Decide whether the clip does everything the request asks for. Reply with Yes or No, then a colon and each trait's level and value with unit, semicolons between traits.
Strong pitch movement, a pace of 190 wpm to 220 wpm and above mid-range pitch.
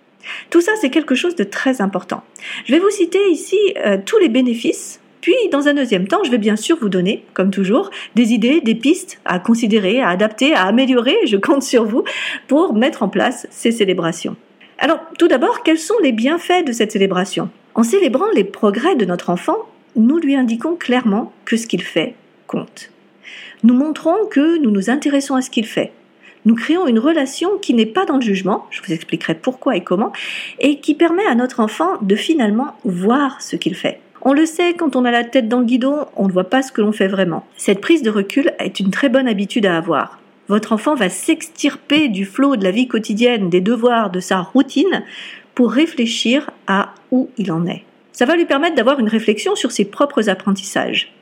Yes: wide, 6.6 semitones; average, 210 wpm; very high, 250 Hz